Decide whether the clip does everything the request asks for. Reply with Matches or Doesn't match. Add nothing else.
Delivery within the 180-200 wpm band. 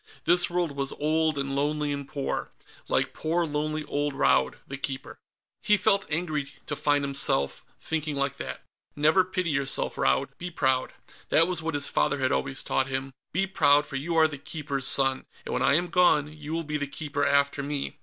Matches